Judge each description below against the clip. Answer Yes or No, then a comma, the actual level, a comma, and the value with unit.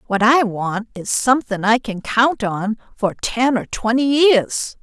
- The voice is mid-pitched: No, high, 230 Hz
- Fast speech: No, average, 175 wpm